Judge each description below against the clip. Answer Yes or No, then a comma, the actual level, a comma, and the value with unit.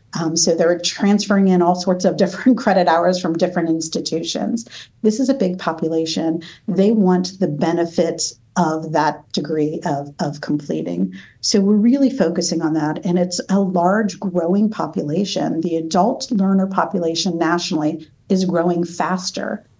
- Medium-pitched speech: Yes, medium, 175 Hz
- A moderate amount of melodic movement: Yes, average, 3.1 semitones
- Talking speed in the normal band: Yes, average, 150 wpm